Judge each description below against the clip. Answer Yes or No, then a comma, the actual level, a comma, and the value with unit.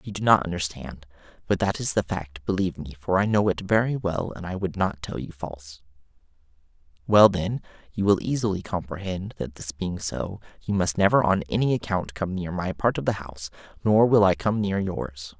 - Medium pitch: No, very low, 90 Hz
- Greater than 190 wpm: Yes, fast, 205 wpm